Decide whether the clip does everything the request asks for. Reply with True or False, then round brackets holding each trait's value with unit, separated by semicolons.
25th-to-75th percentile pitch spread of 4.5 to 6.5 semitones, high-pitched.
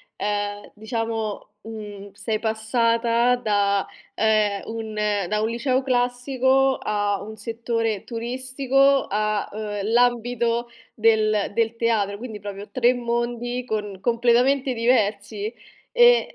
False (2.6 semitones; 225 Hz)